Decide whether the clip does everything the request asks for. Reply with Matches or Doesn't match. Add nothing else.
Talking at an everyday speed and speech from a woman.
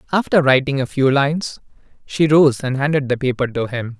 Doesn't match